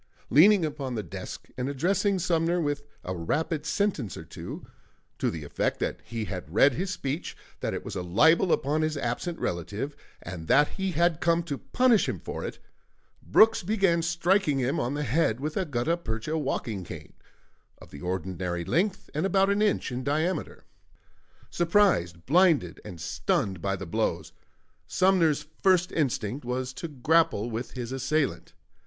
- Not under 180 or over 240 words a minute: No, average, 165 wpm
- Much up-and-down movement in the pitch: Yes, wide, 7.2 semitones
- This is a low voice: No, medium, 145 Hz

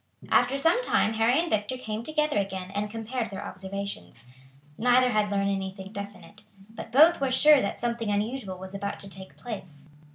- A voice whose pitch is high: Yes, high, 215 Hz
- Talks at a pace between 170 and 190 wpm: Yes, average, 175 wpm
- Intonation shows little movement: No, average, 4.1 semitones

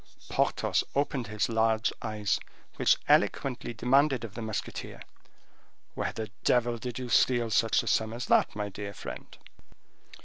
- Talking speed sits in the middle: Yes, average, 145 wpm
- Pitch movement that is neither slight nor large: No, narrow, 2.1 semitones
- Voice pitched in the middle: No, low, 115 Hz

